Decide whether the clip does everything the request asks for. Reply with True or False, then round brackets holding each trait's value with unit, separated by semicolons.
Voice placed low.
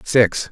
True (115 Hz)